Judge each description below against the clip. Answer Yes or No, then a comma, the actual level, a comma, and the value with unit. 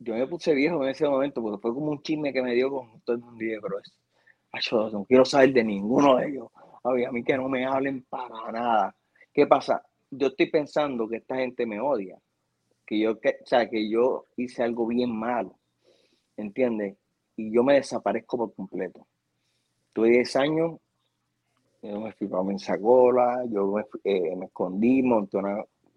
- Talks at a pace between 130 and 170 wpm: No, average, 185 wpm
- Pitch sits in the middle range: No, low, 120 Hz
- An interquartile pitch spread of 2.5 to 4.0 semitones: Yes, average, 3.4 semitones